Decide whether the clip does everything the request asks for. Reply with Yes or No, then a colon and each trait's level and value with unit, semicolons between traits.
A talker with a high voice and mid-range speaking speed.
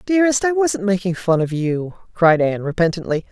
Yes: high, 195 Hz; average, 180 wpm